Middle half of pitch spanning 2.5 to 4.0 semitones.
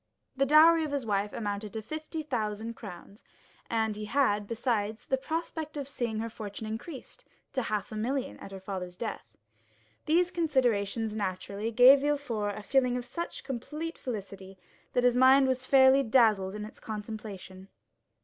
No: average, 4.6 semitones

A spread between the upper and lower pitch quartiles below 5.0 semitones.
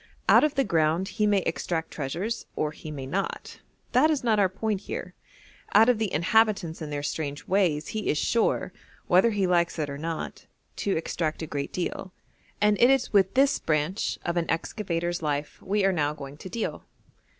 No: average, 5.3 semitones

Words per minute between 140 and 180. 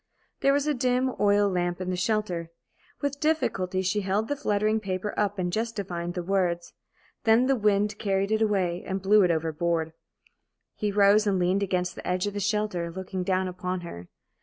No: average, 190 wpm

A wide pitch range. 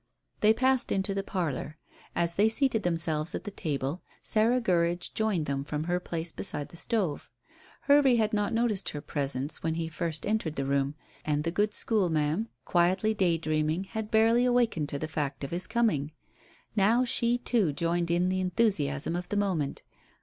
Yes: wide, 5.8 semitones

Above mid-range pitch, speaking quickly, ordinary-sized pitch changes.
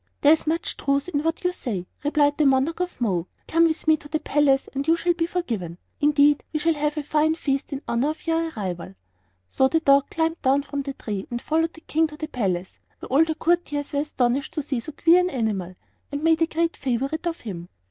Yes: very high, 295 Hz; fast, 235 wpm; average, 3.6 semitones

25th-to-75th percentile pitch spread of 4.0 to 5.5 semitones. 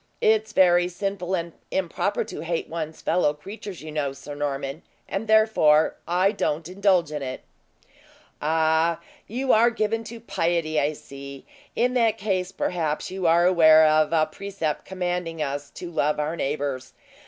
Yes: average, 4.4 semitones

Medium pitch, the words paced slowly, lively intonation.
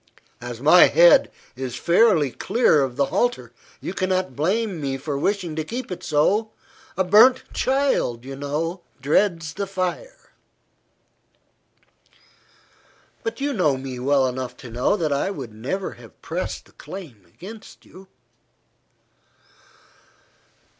Yes: medium, 170 Hz; slow, 130 wpm; wide, 7.0 semitones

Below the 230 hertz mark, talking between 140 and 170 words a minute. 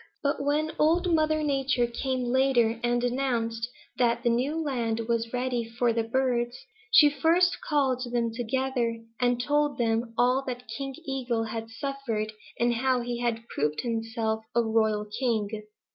No: high, 245 Hz; average, 155 wpm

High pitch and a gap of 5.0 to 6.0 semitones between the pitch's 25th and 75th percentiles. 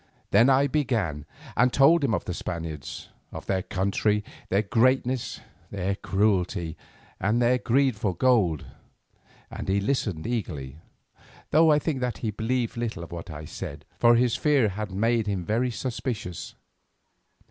No: low, 110 Hz; average, 5.3 semitones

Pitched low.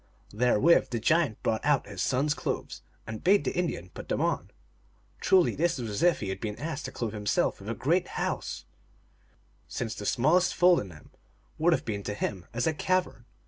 Yes: low, 125 Hz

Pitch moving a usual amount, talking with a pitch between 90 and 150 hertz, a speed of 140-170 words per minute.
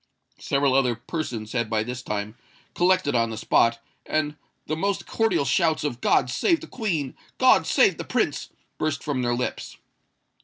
Yes: average, 4.9 semitones; low, 135 Hz; average, 165 wpm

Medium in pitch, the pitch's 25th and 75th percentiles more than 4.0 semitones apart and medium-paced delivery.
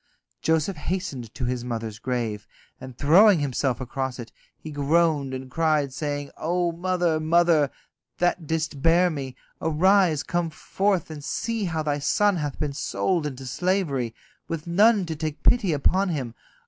Yes: medium, 155 Hz; average, 4.5 semitones; average, 155 wpm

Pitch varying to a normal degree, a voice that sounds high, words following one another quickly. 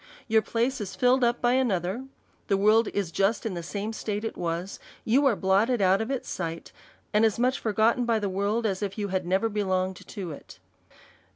Yes: average, 3.4 semitones; high, 210 Hz; fast, 210 wpm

